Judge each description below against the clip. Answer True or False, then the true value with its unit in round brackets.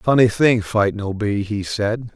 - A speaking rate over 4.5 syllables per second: False (3.8 syllables/s)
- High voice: False (110 Hz)